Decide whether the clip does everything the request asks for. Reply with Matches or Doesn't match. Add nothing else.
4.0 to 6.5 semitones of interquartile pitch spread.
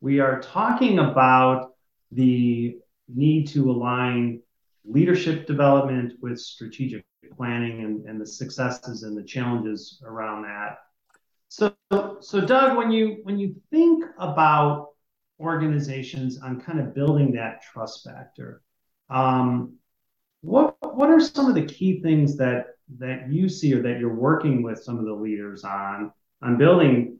Matches